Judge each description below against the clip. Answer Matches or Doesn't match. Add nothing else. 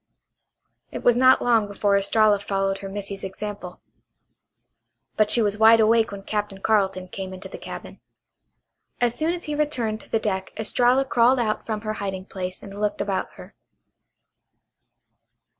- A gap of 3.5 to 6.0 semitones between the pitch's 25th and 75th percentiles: Doesn't match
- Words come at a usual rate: Matches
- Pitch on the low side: Doesn't match